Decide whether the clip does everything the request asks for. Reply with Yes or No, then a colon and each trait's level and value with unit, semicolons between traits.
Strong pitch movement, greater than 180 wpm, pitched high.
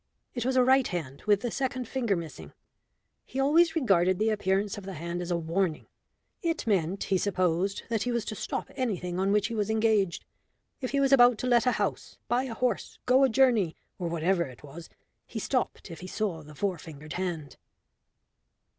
Yes: wide, 5.9 semitones; average, 200 wpm; high, 200 Hz